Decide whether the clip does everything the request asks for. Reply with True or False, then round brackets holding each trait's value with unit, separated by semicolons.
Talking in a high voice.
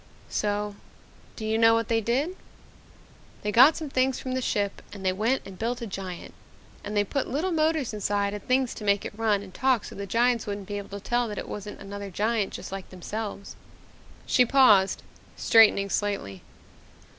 True (210 Hz)